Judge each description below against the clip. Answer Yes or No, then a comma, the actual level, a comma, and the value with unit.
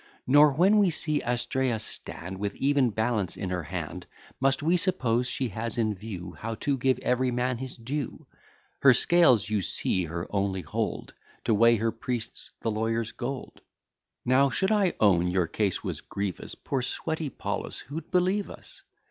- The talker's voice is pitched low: Yes, low, 120 Hz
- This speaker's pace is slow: No, average, 170 wpm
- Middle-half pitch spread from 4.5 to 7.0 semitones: Yes, average, 5.2 semitones